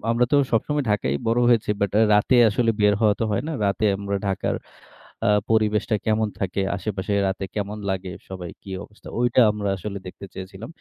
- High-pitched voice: No, low, 105 Hz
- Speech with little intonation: Yes, narrow, 2.3 semitones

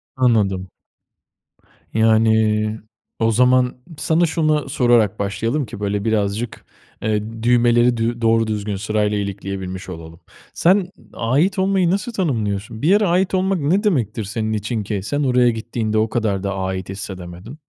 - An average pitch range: Yes, average, 3.9 semitones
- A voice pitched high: No, low, 110 Hz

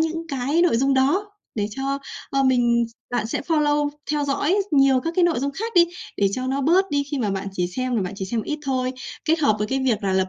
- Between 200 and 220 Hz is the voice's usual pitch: No, very high, 270 Hz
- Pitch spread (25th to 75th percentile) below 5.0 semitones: Yes, average, 4.4 semitones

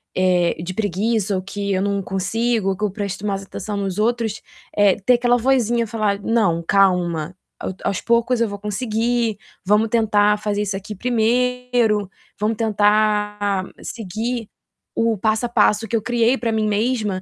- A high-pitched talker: Yes, high, 210 Hz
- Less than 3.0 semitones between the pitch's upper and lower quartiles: Yes, narrow, 2.6 semitones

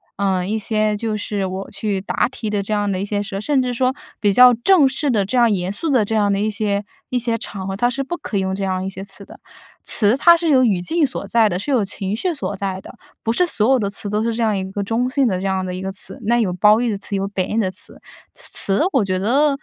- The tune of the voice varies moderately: Yes, average, 3.8 semitones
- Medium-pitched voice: No, high, 210 Hz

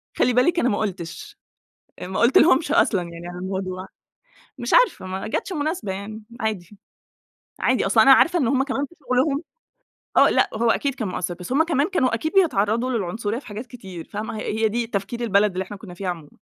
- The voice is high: Yes, high, 220 Hz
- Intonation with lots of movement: Yes, wide, 5.7 semitones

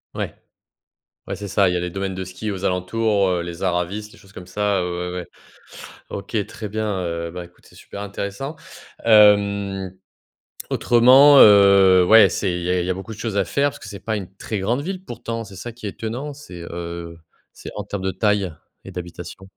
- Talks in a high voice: No, low, 100 Hz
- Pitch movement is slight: No, average, 3.1 semitones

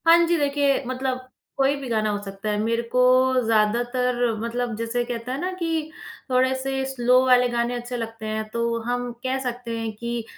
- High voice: Yes, high, 245 Hz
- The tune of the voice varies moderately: No, narrow, 2.2 semitones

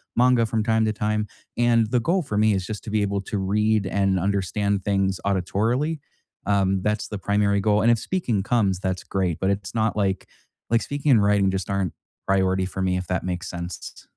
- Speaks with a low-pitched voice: Yes, low, 100 Hz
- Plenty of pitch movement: No, narrow, 2.4 semitones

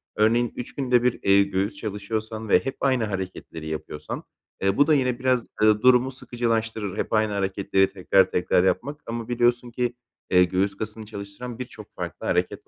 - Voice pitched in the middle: No, low, 110 Hz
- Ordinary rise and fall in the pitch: Yes, average, 3.7 semitones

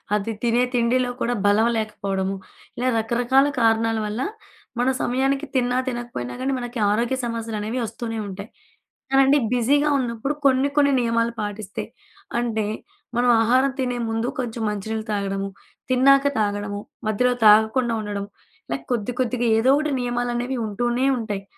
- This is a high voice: Yes, high, 235 Hz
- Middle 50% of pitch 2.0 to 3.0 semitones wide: Yes, average, 2.7 semitones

